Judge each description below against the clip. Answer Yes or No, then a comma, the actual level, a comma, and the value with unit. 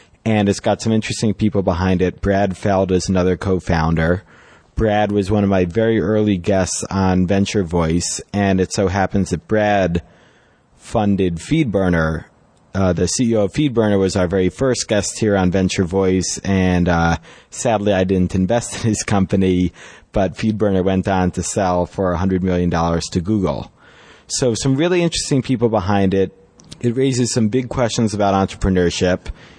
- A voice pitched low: Yes, very low, 95 Hz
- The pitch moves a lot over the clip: No, average, 3.0 semitones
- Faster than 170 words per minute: No, average, 165 wpm